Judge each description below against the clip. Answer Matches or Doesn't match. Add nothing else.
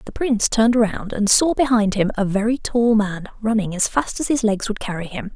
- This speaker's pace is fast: Matches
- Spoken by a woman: Matches